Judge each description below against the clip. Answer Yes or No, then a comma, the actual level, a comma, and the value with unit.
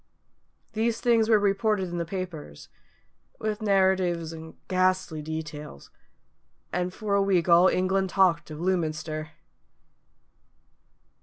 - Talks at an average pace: No, slow, 110 wpm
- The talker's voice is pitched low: No, medium, 185 Hz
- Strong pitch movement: No, average, 3.5 semitones